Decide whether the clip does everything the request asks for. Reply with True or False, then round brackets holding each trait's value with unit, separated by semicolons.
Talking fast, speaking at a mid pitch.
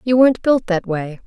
False (235 wpm; 215 Hz)